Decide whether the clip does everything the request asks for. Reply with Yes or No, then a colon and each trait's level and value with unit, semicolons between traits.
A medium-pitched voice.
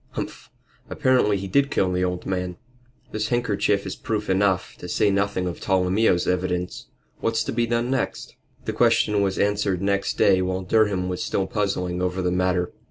No: very low, 95 Hz